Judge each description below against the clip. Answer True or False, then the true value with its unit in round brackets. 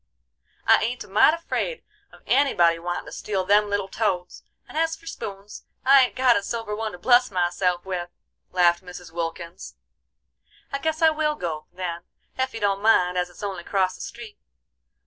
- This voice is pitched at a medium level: False (200 Hz)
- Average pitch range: False (5.8 semitones)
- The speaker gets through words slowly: False (185 wpm)